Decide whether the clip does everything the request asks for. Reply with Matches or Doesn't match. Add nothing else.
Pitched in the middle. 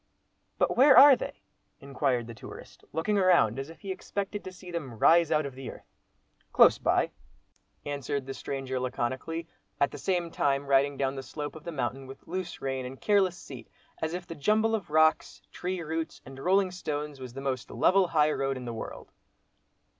Matches